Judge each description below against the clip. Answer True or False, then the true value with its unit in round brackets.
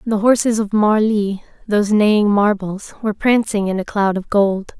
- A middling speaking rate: True (175 wpm)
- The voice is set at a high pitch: True (210 Hz)